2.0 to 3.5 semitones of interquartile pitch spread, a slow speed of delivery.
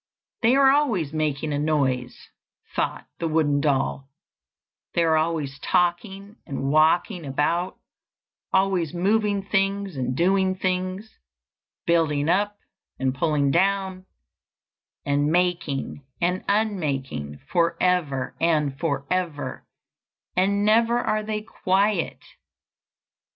No: average, 5.0 semitones; slow, 110 wpm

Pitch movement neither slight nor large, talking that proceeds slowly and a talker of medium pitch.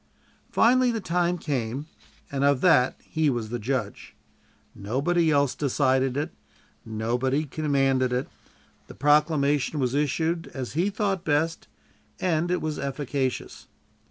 Yes: average, 3.8 semitones; slow, 130 wpm; medium, 145 Hz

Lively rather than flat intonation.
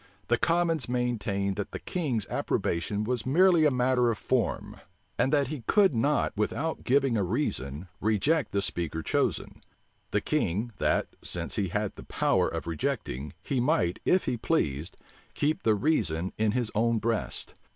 Yes: wide, 6.3 semitones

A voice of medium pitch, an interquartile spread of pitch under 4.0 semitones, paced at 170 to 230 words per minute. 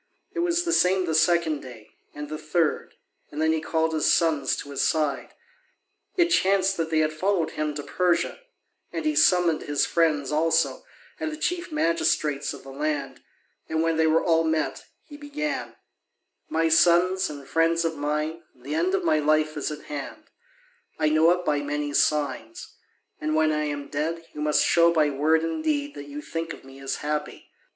Yes: medium, 160 Hz; narrow, 2.4 semitones; average, 190 wpm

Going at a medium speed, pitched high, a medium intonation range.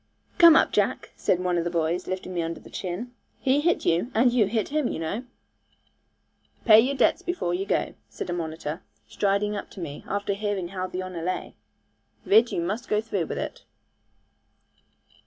Yes: average, 190 wpm; high, 195 Hz; average, 4.6 semitones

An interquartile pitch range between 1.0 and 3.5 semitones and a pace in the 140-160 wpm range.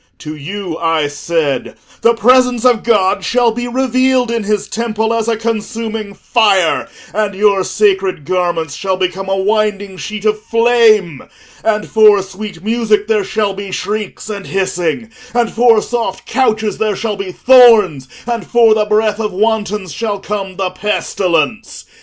Yes: average, 3.0 semitones; average, 155 wpm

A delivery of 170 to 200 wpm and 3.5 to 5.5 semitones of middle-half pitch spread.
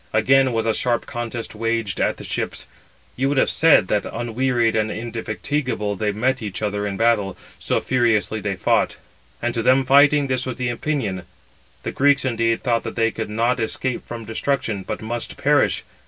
No: average, 185 wpm; average, 3.0 semitones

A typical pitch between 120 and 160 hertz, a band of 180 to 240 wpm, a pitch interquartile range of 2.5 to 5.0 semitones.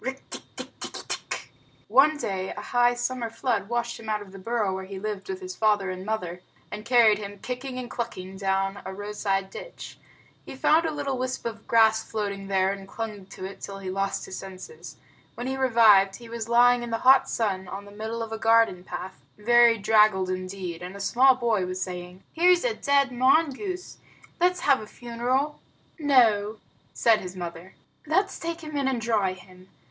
No: high, 220 Hz; average, 185 wpm; average, 4.6 semitones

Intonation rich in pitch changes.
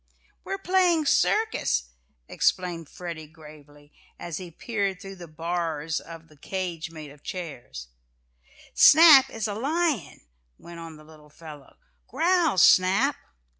Yes: wide, 6.5 semitones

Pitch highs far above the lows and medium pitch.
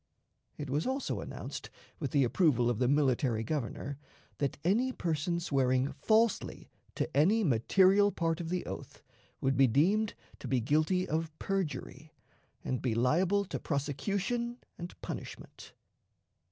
Yes: wide, 6.0 semitones; medium, 155 Hz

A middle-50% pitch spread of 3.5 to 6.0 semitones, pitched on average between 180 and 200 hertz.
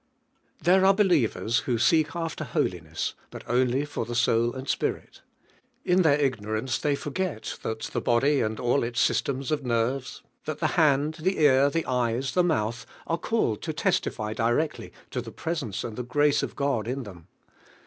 No: average, 4.8 semitones; low, 130 Hz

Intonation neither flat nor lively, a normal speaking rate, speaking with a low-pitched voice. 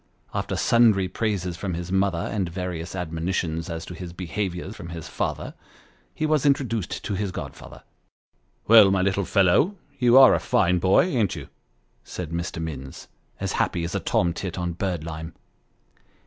Yes: average, 3.3 semitones; average, 165 wpm; very low, 90 Hz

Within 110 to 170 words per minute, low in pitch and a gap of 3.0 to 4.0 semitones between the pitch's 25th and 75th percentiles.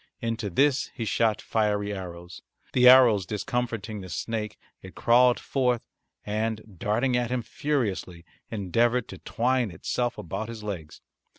Yes: slow, 135 wpm; low, 110 Hz; average, 3.3 semitones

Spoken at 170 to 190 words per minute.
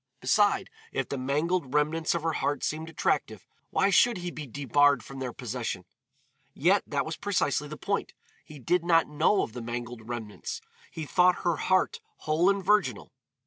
Yes: average, 175 wpm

